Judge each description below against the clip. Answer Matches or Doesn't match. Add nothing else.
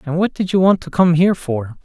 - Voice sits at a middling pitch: Matches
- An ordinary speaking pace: Doesn't match